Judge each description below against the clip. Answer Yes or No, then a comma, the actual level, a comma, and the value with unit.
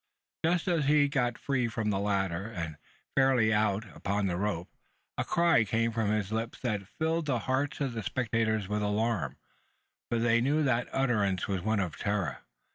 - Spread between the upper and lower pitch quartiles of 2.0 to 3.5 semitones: No, average, 4.3 semitones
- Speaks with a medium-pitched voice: No, low, 110 Hz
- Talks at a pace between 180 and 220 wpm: Yes, average, 190 wpm